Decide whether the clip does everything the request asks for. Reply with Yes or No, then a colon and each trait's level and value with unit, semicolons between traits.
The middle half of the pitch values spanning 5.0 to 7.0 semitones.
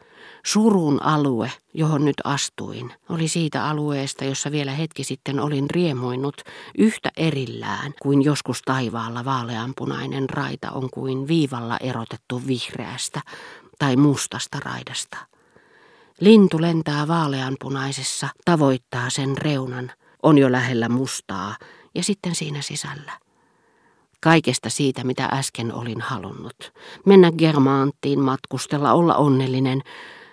No: average, 3.0 semitones